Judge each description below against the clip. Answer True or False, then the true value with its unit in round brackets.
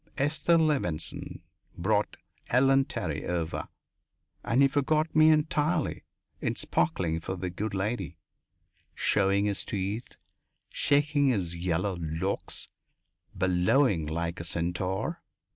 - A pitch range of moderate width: False (7.9 semitones)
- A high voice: False (100 Hz)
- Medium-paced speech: False (110 wpm)